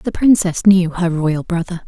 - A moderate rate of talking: Yes, average, 190 wpm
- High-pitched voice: No, medium, 180 Hz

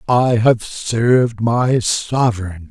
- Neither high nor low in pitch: No, low, 115 Hz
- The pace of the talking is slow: Yes, slow, 110 wpm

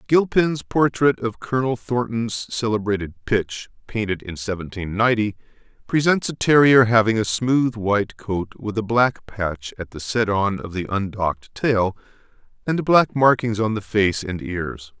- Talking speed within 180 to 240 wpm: No, average, 155 wpm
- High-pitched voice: No, low, 110 Hz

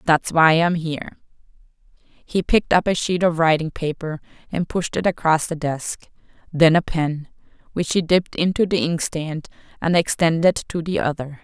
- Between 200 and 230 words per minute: No, average, 165 wpm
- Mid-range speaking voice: Yes, medium, 165 Hz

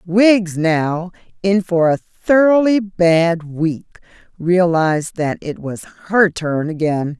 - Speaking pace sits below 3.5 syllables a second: Yes, 3.2 syllables/s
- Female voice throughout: Yes, female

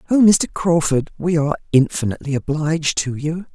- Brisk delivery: No, average, 150 wpm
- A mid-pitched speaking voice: Yes, medium, 155 Hz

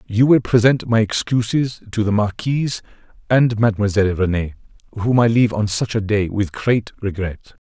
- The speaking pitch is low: Yes, low, 110 Hz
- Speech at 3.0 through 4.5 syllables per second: No, 5.3 syllables/s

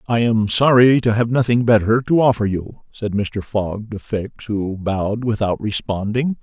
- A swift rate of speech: No, average, 175 wpm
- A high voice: No, low, 110 Hz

